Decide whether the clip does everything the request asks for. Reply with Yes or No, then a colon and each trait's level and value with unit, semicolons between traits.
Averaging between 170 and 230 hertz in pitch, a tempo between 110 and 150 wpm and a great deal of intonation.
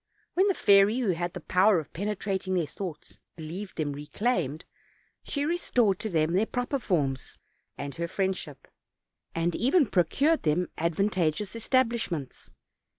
Yes: medium, 185 Hz; average, 140 wpm; wide, 5.7 semitones